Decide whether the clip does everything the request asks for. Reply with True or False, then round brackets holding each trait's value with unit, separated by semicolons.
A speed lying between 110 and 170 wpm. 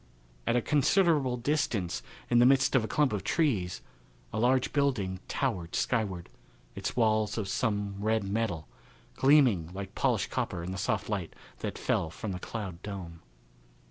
True (160 wpm)